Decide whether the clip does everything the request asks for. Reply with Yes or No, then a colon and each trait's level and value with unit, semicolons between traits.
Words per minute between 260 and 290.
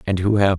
No: fast, 305 wpm